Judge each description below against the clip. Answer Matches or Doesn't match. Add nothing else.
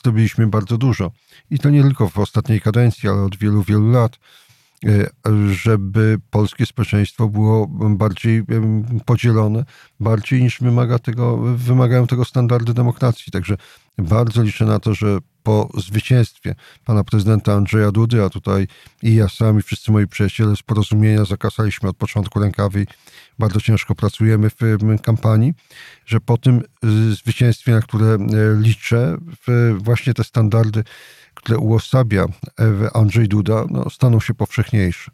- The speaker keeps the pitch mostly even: Matches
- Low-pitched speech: Matches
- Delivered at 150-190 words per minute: Doesn't match